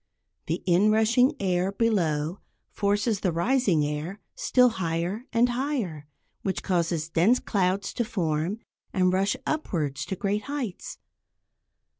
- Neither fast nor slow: No, slow, 120 wpm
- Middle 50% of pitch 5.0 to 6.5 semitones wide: Yes, average, 5.3 semitones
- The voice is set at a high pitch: Yes, high, 195 Hz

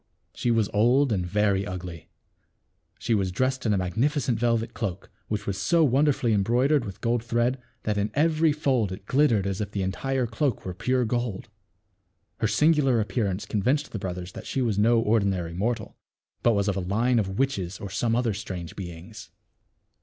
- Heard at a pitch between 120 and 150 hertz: No, low, 110 Hz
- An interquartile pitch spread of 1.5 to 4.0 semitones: No, average, 4.4 semitones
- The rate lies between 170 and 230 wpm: Yes, average, 185 wpm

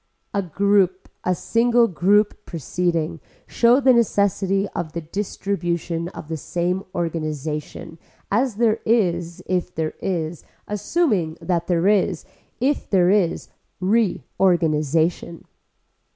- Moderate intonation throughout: Yes, average, 3.6 semitones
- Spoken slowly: Yes, slow, 110 wpm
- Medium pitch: Yes, medium, 180 Hz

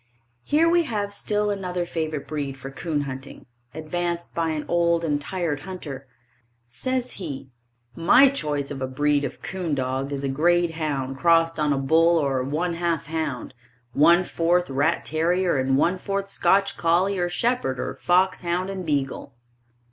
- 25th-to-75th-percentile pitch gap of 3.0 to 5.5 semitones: Yes, average, 4.1 semitones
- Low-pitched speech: No, medium, 165 Hz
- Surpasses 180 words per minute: No, average, 165 wpm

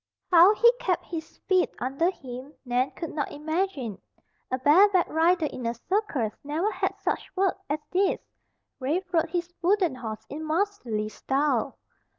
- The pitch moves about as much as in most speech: No, wide, 5.9 semitones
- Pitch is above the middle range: Yes, very high, 315 Hz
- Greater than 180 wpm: No, average, 155 wpm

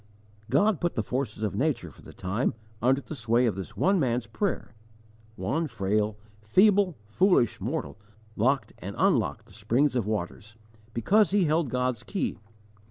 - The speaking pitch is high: No, low, 125 Hz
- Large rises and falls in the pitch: Yes, wide, 7.0 semitones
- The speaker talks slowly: No, average, 160 wpm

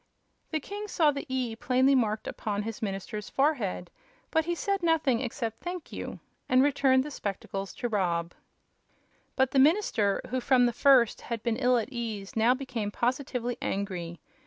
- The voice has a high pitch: Yes, high, 245 Hz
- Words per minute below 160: No, average, 165 wpm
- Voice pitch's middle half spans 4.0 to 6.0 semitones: Yes, average, 4.6 semitones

